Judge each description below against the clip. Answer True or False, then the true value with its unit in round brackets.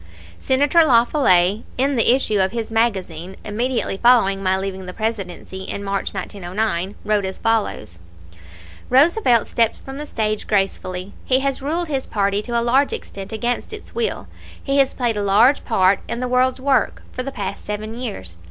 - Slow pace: False (180 wpm)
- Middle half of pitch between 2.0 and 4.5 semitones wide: False (4.9 semitones)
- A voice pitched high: True (220 Hz)